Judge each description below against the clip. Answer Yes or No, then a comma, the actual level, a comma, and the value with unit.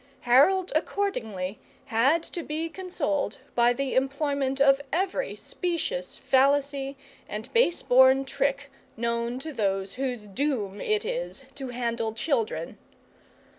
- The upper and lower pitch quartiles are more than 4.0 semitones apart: Yes, average, 4.6 semitones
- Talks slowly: Yes, slow, 120 wpm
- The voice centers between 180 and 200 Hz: No, very high, 270 Hz